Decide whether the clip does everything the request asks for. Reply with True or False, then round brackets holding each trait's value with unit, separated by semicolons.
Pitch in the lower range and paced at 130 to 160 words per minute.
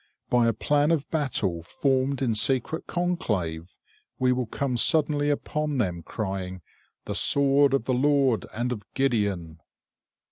True (125 Hz; 140 wpm)